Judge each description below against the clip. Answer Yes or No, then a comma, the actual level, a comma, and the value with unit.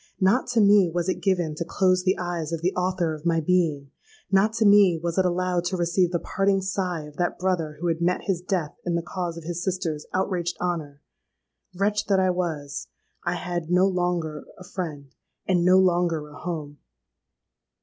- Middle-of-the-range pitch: Yes, medium, 175 Hz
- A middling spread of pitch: No, narrow, 2.2 semitones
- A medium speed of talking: Yes, average, 190 wpm